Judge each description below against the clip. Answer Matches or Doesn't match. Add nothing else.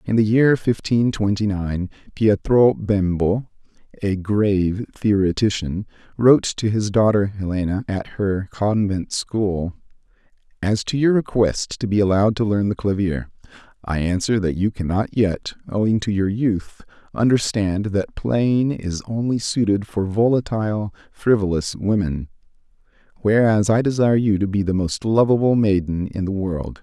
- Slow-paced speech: Doesn't match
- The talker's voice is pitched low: Matches